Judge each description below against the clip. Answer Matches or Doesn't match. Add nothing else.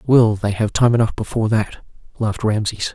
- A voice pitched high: Doesn't match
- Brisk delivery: Doesn't match